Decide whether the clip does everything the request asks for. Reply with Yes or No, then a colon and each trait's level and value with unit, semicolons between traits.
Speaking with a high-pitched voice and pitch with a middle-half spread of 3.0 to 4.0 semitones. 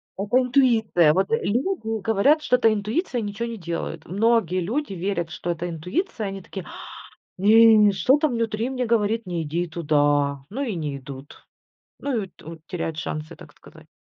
No: high, 205 Hz; wide, 5.4 semitones